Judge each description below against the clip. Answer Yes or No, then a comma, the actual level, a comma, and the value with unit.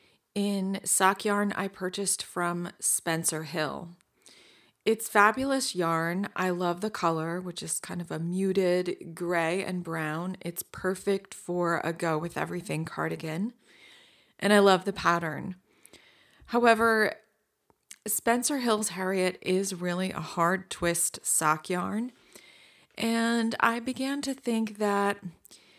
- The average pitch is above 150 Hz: Yes, medium, 185 Hz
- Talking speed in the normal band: No, slow, 125 wpm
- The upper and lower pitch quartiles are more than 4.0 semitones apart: No, average, 3.5 semitones